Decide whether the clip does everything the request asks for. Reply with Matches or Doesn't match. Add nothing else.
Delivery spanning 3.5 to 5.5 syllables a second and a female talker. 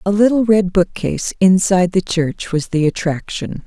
Matches